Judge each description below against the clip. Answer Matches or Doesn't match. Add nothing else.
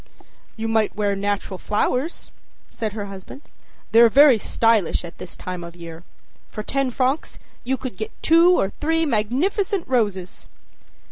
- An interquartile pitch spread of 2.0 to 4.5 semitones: Doesn't match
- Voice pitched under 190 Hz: Doesn't match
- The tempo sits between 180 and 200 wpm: Doesn't match